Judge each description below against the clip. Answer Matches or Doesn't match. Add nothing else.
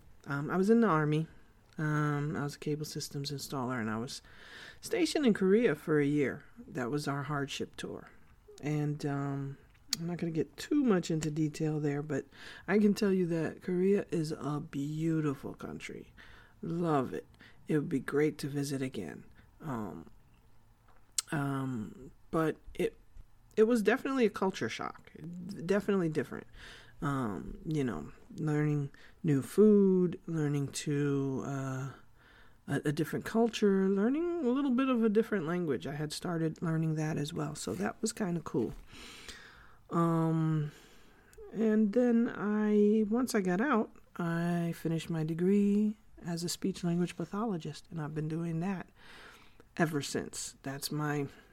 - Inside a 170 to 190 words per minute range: Doesn't match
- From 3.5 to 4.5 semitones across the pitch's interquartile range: Doesn't match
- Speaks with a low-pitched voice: Doesn't match